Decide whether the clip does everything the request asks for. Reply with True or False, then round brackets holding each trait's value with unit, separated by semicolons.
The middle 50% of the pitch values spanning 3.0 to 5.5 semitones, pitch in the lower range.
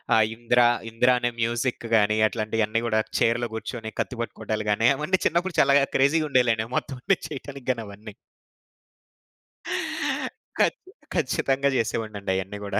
True (3.7 semitones; 120 Hz)